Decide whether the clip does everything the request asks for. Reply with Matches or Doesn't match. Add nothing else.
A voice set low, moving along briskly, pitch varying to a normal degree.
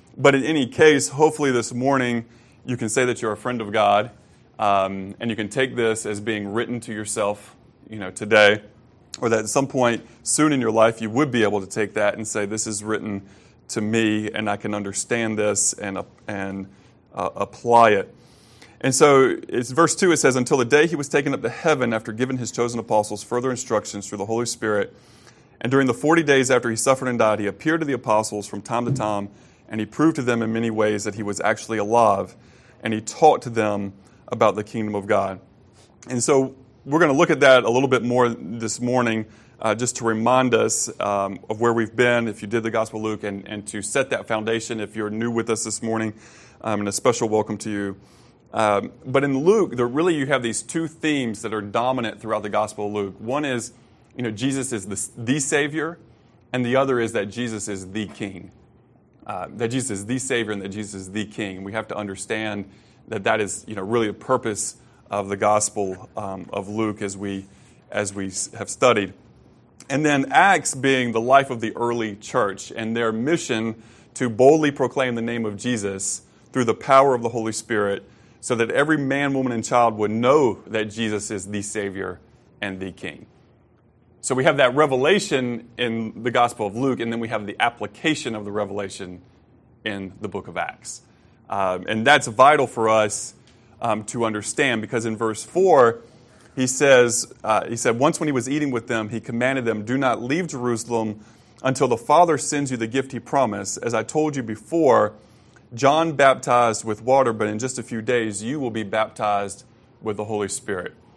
Matches